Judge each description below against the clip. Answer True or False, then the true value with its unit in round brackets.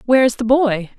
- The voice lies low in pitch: False (240 Hz)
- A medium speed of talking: False (245 wpm)